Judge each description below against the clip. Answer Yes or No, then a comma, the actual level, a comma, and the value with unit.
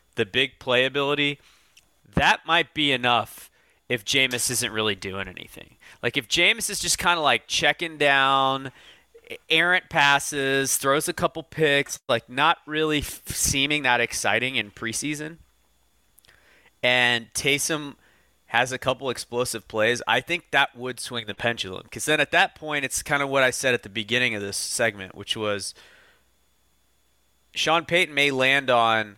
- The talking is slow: No, average, 155 wpm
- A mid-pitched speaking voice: No, low, 130 Hz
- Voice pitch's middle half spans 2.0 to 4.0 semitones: No, average, 4.6 semitones